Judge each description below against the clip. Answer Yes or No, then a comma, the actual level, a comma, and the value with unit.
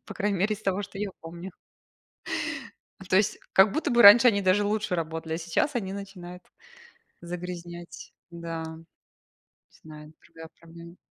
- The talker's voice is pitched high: No, medium, 180 Hz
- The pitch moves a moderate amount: Yes, average, 3.3 semitones